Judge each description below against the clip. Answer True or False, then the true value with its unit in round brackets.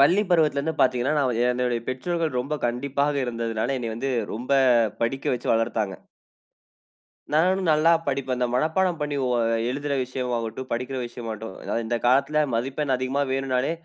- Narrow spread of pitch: False (3.3 semitones)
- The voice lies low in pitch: True (130 Hz)